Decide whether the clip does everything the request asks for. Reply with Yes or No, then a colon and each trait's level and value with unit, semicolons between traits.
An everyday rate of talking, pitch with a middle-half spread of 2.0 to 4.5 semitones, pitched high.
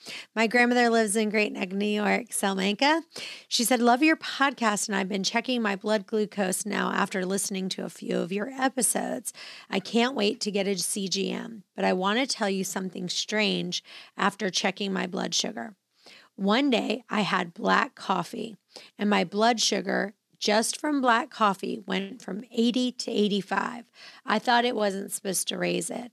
Yes: average, 175 wpm; average, 3.1 semitones; high, 210 Hz